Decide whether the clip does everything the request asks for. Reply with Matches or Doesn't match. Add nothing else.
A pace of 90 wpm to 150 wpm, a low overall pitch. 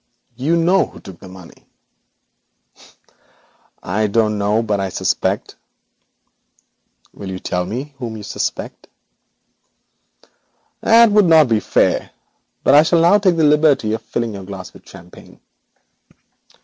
Matches